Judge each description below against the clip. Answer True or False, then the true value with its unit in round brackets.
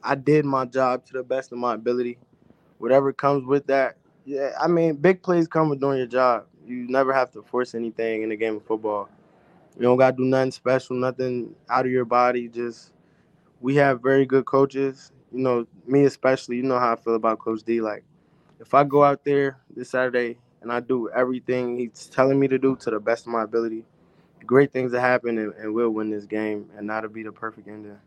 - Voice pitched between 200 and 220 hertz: False (125 Hz)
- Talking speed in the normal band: False (220 wpm)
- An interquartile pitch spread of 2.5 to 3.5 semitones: True (2.8 semitones)